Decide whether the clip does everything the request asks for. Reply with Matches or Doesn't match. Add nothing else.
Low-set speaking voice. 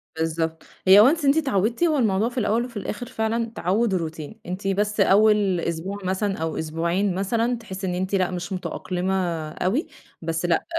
Doesn't match